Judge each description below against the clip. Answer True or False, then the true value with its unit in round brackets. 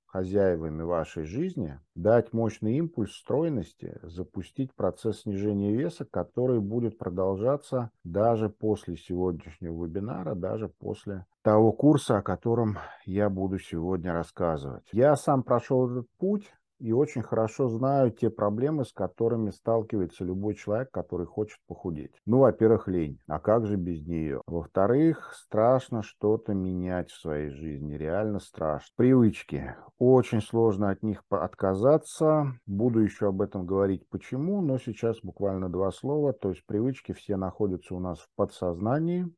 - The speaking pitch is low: True (105 Hz)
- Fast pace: False (135 wpm)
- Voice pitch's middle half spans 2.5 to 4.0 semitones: False (4.8 semitones)